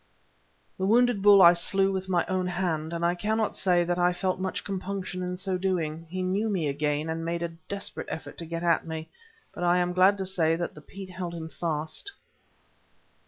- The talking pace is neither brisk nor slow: No, fast, 210 wpm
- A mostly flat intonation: Yes, narrow, 2.3 semitones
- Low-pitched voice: No, medium, 180 Hz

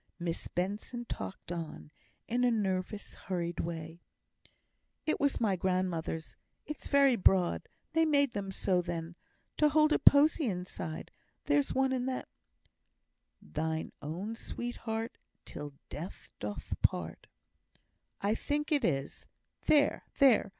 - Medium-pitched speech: No, high, 200 Hz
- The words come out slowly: Yes, slow, 125 wpm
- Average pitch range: No, wide, 7.7 semitones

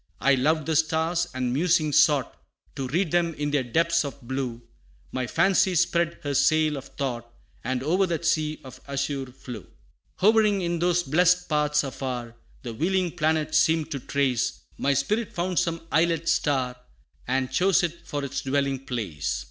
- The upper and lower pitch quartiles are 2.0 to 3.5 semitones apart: No, average, 4.2 semitones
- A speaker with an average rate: Yes, average, 165 wpm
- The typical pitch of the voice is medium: Yes, medium, 150 Hz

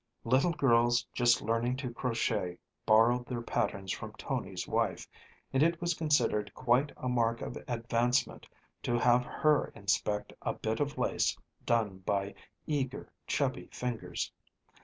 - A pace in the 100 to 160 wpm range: Yes, average, 140 wpm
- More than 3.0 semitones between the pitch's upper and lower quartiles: No, narrow, 2.6 semitones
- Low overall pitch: Yes, low, 120 Hz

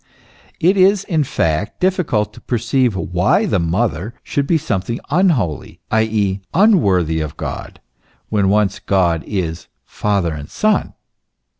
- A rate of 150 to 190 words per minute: No, slow, 135 wpm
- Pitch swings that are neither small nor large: No, wide, 8.3 semitones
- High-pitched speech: No, low, 105 Hz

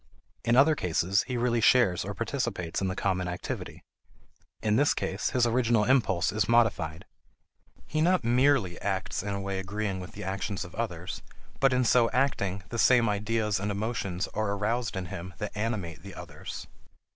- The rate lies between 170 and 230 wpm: Yes, average, 175 wpm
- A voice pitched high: No, low, 105 Hz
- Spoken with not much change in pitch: No, average, 4.0 semitones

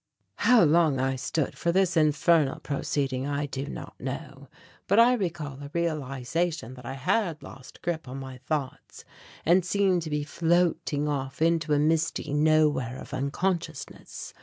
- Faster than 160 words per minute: No, average, 155 wpm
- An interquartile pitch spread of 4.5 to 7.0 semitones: No, average, 3.8 semitones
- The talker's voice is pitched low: No, medium, 150 Hz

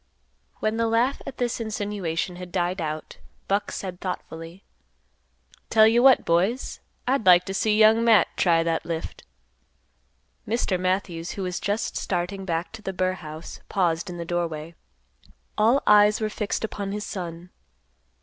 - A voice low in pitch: No, high, 190 Hz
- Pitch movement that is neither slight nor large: Yes, average, 3.9 semitones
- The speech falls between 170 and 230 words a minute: No, average, 155 wpm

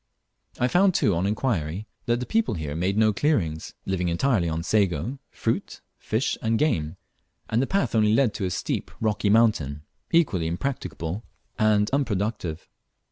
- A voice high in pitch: No, low, 105 Hz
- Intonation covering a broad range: Yes, wide, 6.0 semitones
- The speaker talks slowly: No, average, 155 wpm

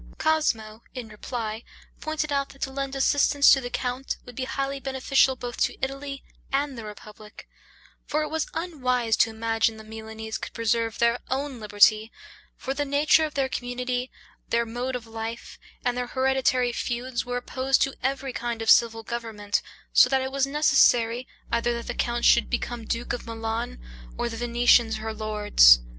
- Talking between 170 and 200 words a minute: Yes, average, 175 wpm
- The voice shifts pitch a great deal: No, average, 3.0 semitones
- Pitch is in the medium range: No, high, 245 Hz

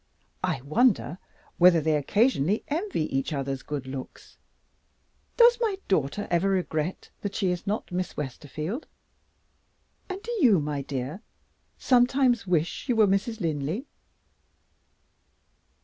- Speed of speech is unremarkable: No, slow, 125 wpm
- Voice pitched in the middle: Yes, medium, 180 Hz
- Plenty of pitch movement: Yes, wide, 7.8 semitones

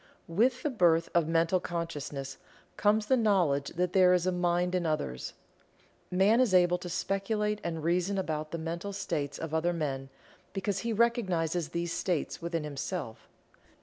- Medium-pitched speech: Yes, medium, 175 Hz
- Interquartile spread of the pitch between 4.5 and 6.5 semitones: No, average, 3.2 semitones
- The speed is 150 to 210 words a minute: Yes, average, 160 wpm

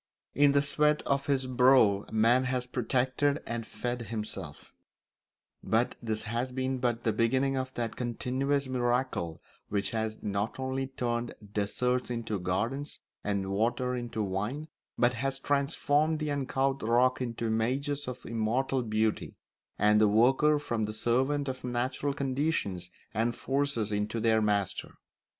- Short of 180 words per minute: Yes, average, 140 wpm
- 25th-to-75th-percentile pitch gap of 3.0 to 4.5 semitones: Yes, average, 3.4 semitones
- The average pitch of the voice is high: No, low, 125 Hz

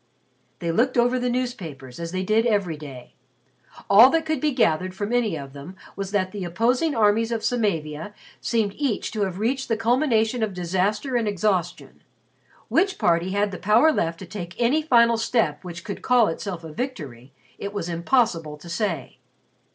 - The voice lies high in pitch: Yes, high, 205 Hz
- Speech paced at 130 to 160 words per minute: No, average, 180 wpm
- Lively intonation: Yes, wide, 5.7 semitones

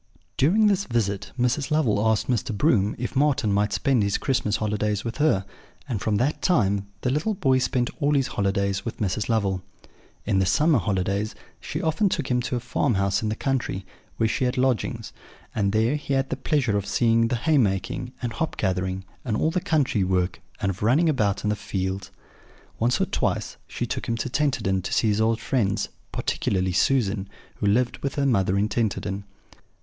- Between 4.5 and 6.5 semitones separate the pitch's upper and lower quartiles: Yes, average, 5.1 semitones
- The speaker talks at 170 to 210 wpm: Yes, average, 190 wpm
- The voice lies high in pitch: No, low, 110 Hz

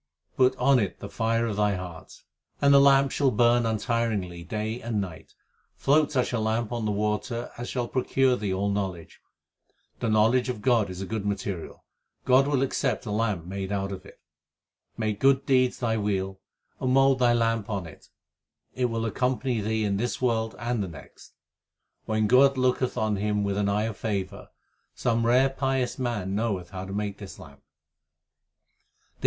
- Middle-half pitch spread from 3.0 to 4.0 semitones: Yes, average, 3.7 semitones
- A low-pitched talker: Yes, low, 110 Hz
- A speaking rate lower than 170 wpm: No, average, 180 wpm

